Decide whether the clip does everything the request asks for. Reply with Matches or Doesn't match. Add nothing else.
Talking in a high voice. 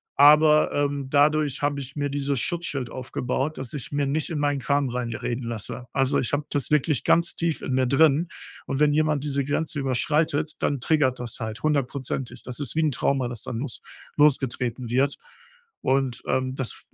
Doesn't match